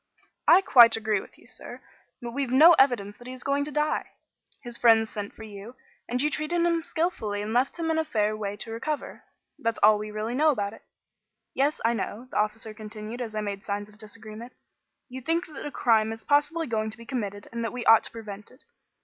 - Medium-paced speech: No, fast, 230 wpm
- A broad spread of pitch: No, average, 4.6 semitones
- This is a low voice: No, high, 230 Hz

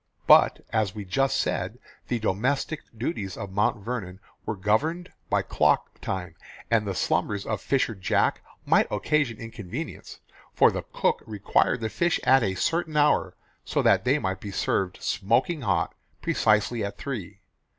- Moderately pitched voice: No, low, 110 Hz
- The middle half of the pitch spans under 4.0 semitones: No, wide, 5.4 semitones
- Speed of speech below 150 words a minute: No, average, 155 wpm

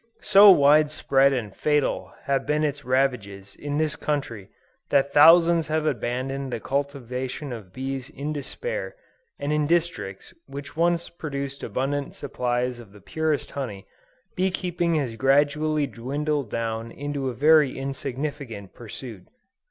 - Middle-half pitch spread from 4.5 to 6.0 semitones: No, average, 3.4 semitones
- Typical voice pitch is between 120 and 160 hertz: Yes, medium, 140 Hz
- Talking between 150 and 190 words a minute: No, slow, 135 wpm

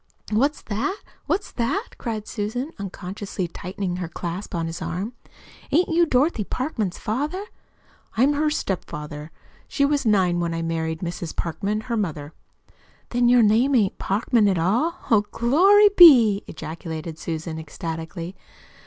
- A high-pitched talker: Yes, high, 205 Hz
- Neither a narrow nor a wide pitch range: No, wide, 7.1 semitones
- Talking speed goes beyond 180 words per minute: No, average, 140 wpm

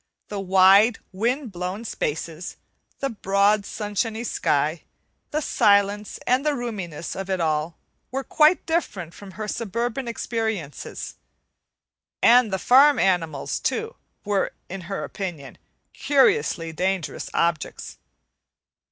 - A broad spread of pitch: No, average, 4.9 semitones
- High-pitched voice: Yes, high, 205 Hz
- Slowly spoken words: Yes, slow, 115 wpm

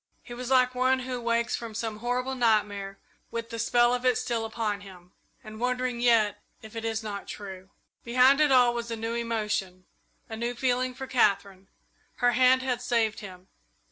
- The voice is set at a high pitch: Yes, high, 235 Hz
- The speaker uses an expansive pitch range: No, average, 2.7 semitones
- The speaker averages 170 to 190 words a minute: Yes, average, 185 wpm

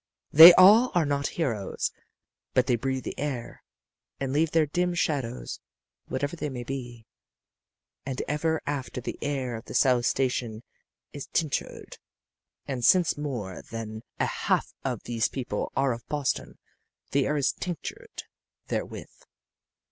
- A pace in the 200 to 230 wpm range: No, average, 140 wpm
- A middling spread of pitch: Yes, average, 3.8 semitones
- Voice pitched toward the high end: No, low, 135 Hz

